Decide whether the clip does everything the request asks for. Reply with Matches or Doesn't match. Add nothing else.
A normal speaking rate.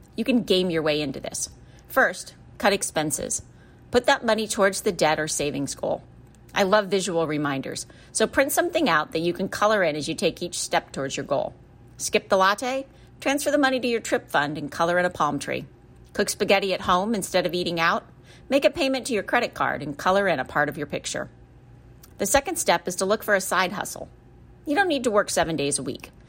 Doesn't match